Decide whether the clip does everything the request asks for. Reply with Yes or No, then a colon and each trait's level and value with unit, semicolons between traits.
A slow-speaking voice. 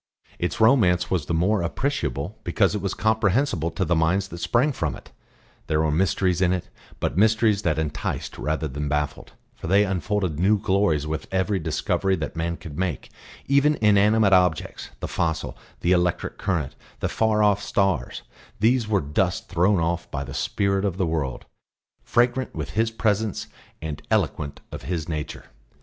No: average, 170 wpm